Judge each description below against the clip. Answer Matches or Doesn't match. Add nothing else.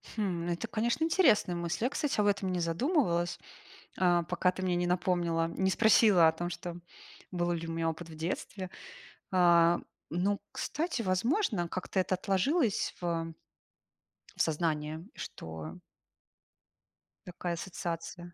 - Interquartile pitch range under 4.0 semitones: Matches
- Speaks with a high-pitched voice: Doesn't match